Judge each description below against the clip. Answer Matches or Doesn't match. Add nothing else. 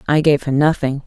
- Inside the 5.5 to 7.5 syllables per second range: Matches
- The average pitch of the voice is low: Doesn't match